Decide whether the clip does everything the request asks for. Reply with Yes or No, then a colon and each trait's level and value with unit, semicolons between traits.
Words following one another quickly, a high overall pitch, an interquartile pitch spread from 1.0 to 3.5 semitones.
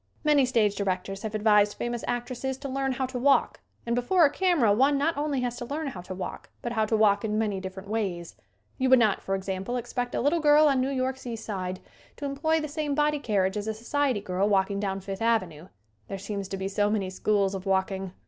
No: fast, 230 wpm; high, 220 Hz; average, 5.3 semitones